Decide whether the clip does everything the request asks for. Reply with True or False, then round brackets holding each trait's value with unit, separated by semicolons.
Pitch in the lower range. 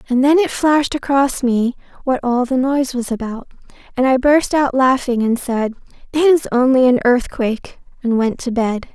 False (255 Hz)